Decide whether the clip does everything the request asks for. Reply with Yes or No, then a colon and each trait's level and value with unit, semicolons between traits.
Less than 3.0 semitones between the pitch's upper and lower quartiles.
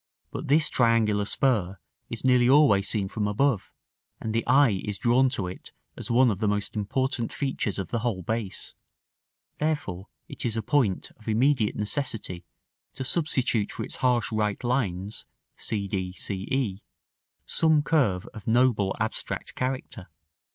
No: average, 4.4 semitones